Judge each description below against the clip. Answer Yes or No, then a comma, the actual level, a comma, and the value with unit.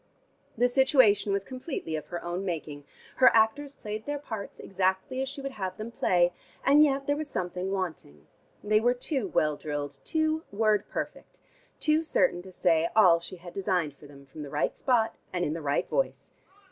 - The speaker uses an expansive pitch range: Yes, wide, 7.3 semitones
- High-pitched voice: Yes, high, 200 Hz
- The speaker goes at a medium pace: Yes, average, 190 wpm